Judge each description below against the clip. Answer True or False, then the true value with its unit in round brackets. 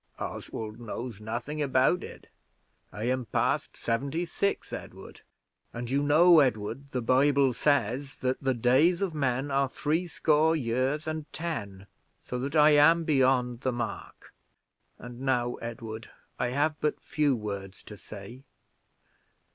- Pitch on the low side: True (130 Hz)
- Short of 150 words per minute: True (140 wpm)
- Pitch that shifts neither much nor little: True (3.9 semitones)